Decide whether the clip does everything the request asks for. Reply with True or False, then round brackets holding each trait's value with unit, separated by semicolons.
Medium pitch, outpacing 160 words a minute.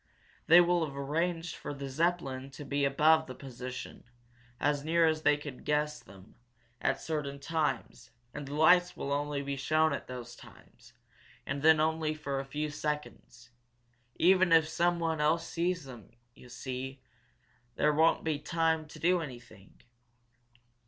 False (150 Hz; 155 wpm)